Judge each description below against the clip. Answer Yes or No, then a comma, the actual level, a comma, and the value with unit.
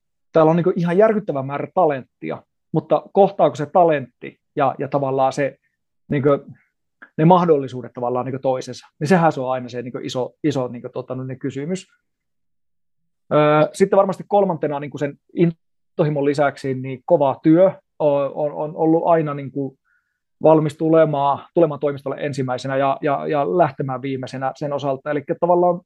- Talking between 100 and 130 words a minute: No, average, 140 wpm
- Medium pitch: Yes, medium, 145 Hz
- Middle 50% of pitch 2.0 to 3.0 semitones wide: No, average, 3.7 semitones